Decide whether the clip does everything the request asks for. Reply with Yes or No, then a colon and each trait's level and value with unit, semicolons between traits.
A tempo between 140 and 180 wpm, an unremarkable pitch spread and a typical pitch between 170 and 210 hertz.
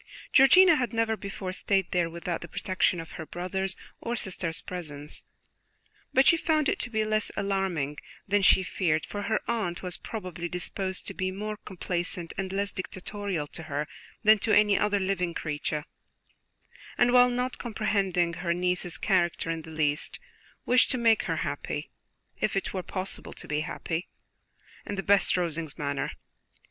Yes: average, 165 wpm; average, 3.7 semitones; medium, 185 Hz